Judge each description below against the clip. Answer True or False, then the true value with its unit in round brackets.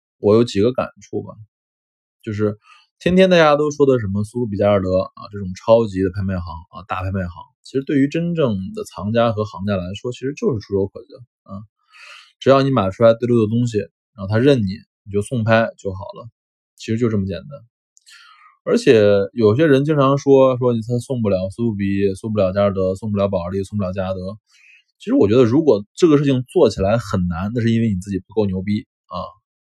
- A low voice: True (105 Hz)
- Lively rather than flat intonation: False (4.0 semitones)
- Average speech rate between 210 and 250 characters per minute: False (310 characters per minute)